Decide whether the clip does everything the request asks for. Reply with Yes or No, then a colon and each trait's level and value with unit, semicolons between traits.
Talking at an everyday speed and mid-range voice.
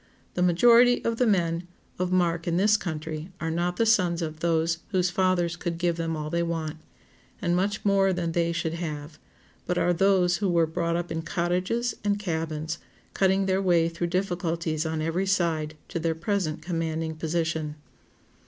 Yes: average, 180 wpm; medium, 170 Hz